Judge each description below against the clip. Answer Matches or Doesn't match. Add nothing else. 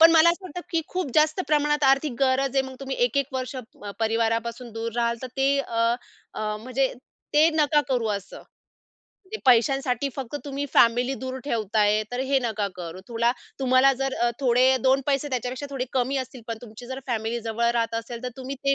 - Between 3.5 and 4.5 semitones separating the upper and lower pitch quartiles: Doesn't match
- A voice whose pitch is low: Doesn't match